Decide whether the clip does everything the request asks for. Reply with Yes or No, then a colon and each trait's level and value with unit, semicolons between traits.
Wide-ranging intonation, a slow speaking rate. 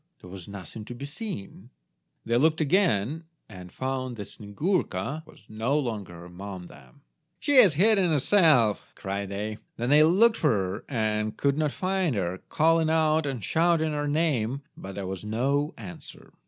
No: wide, 7.7 semitones; average, 165 wpm